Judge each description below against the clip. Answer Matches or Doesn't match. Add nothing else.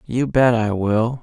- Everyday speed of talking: Matches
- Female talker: Doesn't match